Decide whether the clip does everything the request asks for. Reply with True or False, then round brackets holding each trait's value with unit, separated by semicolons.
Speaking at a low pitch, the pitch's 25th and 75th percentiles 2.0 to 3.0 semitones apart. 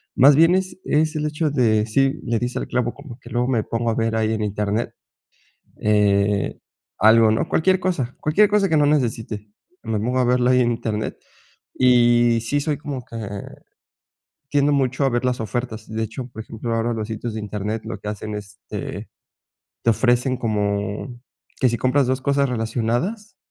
False (120 Hz; 3.8 semitones)